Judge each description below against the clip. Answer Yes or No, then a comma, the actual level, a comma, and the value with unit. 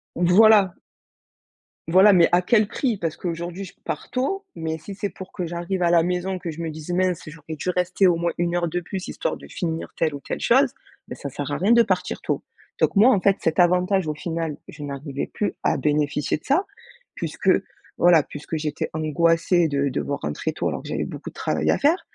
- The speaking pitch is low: No, medium, 175 Hz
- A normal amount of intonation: Yes, average, 3.2 semitones